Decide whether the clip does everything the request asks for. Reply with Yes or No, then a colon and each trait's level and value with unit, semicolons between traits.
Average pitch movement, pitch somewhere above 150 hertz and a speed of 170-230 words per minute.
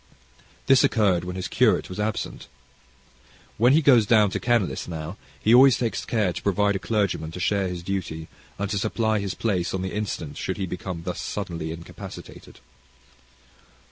No: average, 3.5 semitones; low, 100 Hz; average, 175 wpm